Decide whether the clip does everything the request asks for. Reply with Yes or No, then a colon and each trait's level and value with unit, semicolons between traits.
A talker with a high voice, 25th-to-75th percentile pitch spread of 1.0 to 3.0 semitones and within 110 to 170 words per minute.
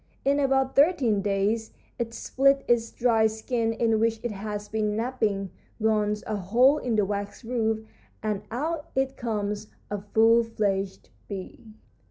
Yes: high, 220 Hz; average, 2.7 semitones; average, 150 wpm